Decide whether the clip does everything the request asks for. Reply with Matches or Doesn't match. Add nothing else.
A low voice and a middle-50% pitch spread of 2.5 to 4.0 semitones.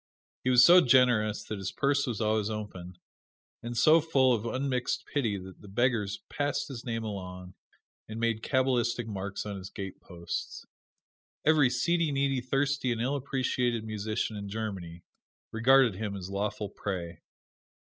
Doesn't match